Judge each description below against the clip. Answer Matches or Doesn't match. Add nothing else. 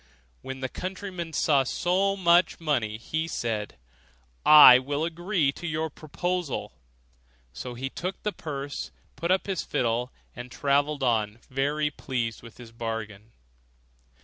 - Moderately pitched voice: Matches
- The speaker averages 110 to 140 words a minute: Matches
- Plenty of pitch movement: Matches